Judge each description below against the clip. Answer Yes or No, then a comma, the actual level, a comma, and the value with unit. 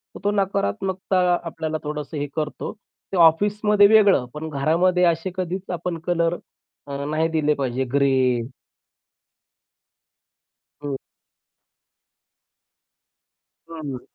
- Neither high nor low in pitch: Yes, medium, 165 Hz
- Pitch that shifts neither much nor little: Yes, average, 4.2 semitones